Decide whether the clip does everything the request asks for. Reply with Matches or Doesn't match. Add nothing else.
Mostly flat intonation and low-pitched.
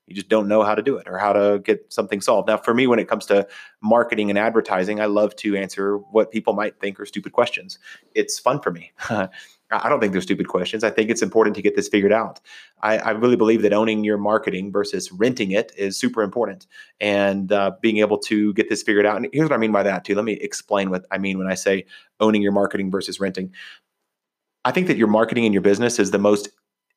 Matches